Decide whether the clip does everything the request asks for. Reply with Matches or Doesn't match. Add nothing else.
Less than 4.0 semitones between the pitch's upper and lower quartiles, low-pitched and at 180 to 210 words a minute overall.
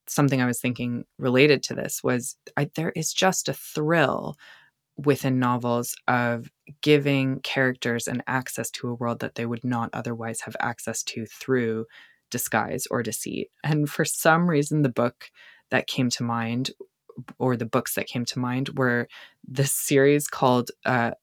Doesn't match